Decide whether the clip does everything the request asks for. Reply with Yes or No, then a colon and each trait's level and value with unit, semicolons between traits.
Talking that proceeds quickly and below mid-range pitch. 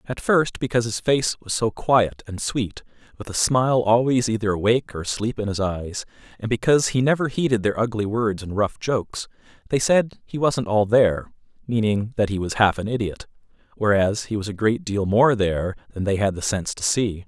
Yes: fast, 210 wpm; low, 110 Hz